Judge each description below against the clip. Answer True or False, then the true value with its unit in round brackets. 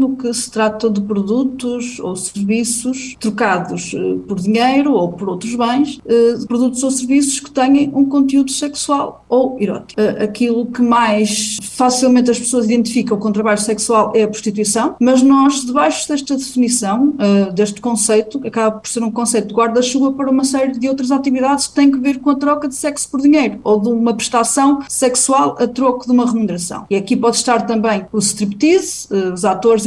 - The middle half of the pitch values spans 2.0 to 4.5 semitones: True (3.7 semitones)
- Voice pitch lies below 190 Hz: False (240 Hz)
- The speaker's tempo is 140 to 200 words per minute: True (180 wpm)